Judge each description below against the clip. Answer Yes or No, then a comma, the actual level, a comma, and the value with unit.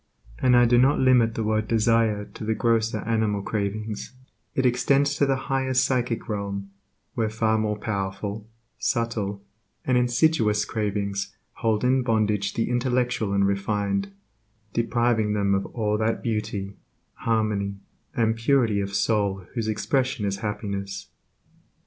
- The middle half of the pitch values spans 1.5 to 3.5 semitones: Yes, average, 2.9 semitones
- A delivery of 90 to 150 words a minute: Yes, slow, 135 wpm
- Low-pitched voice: Yes, low, 110 Hz